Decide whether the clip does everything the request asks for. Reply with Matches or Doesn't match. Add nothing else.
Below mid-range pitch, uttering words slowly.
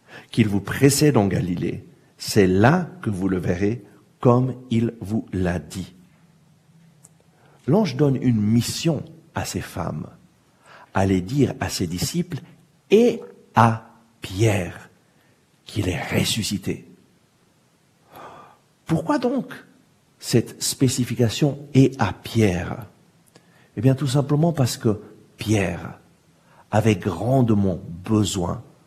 Matches